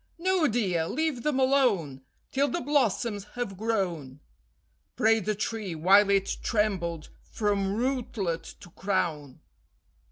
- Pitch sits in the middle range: No, high, 205 Hz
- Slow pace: Yes, slow, 120 wpm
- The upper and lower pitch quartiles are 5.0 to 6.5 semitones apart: Yes, wide, 5.5 semitones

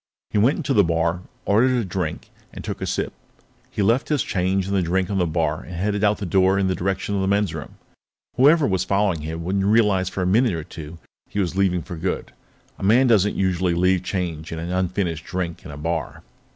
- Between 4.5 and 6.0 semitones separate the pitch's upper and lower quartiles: No, average, 3.0 semitones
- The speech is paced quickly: Yes, fast, 230 wpm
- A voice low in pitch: Yes, very low, 95 Hz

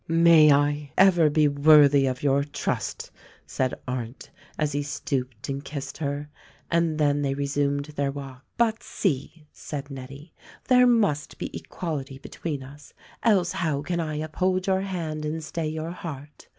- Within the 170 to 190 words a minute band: No, average, 160 wpm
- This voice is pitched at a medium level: Yes, medium, 150 Hz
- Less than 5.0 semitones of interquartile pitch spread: Yes, average, 2.8 semitones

